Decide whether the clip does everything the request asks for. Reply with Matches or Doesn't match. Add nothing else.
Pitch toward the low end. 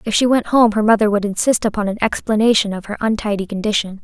Doesn't match